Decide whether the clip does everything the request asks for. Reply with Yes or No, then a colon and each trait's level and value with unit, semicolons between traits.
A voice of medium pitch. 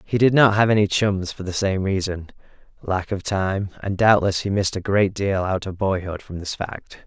No: very low, 95 Hz